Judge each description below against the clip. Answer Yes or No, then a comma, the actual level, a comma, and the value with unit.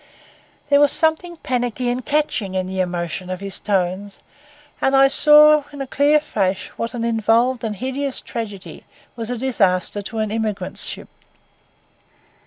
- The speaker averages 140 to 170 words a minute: Yes, average, 155 wpm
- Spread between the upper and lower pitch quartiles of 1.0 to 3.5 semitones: No, wide, 5.4 semitones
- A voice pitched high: Yes, high, 230 Hz